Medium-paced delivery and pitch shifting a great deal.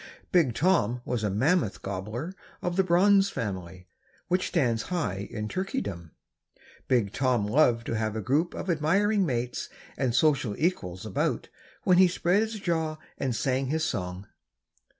Yes: average, 150 wpm; wide, 8.6 semitones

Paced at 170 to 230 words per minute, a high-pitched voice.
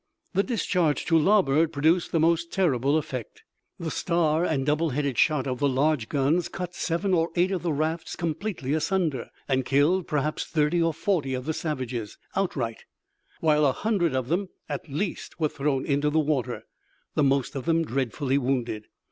No: average, 175 wpm; medium, 155 Hz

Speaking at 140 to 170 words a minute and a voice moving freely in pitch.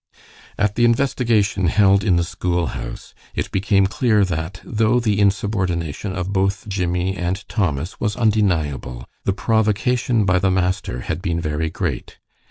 No: average, 150 wpm; average, 3.3 semitones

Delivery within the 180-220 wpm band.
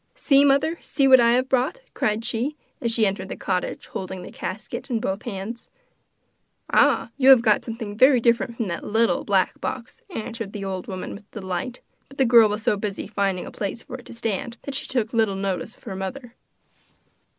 Yes: fast, 205 wpm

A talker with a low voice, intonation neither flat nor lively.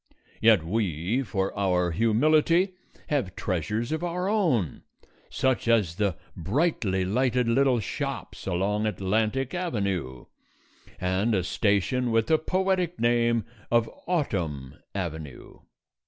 No: low, 110 Hz; wide, 6.2 semitones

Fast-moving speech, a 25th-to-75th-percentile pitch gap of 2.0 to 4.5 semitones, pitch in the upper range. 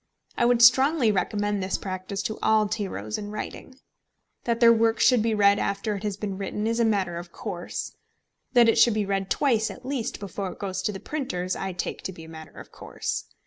Yes: fast, 220 wpm; average, 3.2 semitones; high, 205 Hz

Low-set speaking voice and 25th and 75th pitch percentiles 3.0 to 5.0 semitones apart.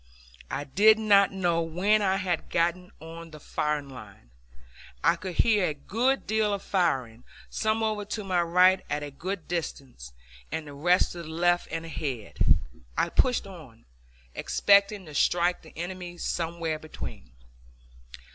No: medium, 175 Hz; average, 4.2 semitones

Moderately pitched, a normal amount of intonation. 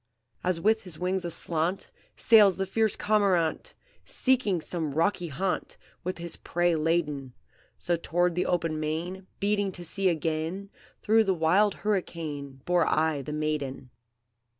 Yes: medium, 175 Hz; average, 3.5 semitones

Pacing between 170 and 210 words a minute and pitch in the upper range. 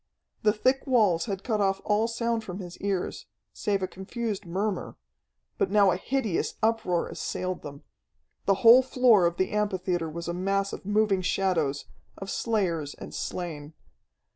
No: average, 160 wpm; high, 195 Hz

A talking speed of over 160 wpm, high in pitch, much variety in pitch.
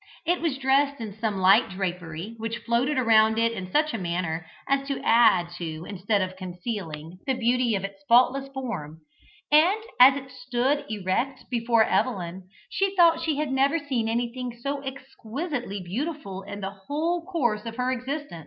Yes: average, 170 wpm; high, 235 Hz; wide, 6.0 semitones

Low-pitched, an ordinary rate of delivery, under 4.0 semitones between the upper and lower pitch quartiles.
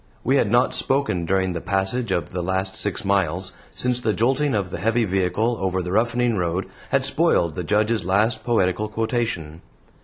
No: low, 100 Hz; average, 180 wpm; average, 4.4 semitones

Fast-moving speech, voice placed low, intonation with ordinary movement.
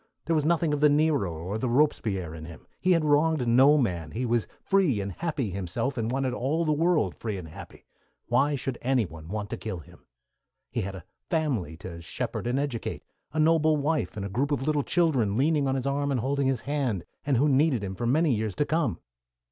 No: fast, 220 wpm; low, 130 Hz; wide, 6.4 semitones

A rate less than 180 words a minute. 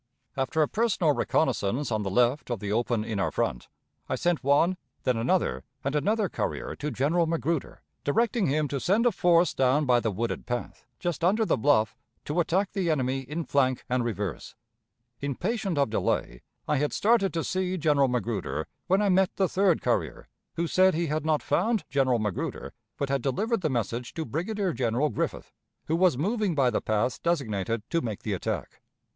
No: average, 185 wpm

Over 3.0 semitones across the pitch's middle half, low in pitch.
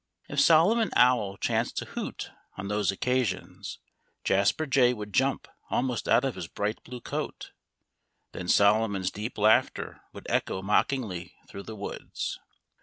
Yes: average, 4.4 semitones; low, 105 Hz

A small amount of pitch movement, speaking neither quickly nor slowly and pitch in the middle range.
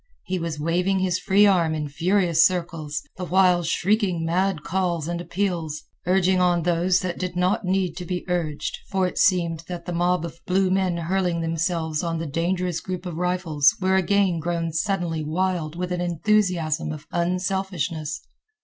Yes: narrow, 2.0 semitones; average, 170 wpm; medium, 175 Hz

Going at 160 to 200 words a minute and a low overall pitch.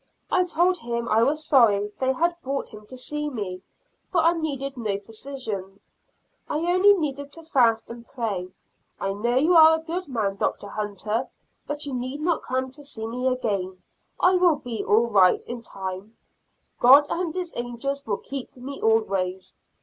No: average, 175 wpm; very high, 255 Hz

